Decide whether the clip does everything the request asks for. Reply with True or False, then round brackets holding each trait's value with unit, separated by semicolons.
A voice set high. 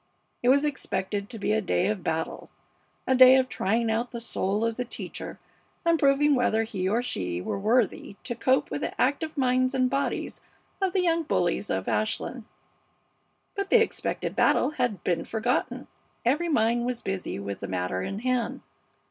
True (240 Hz)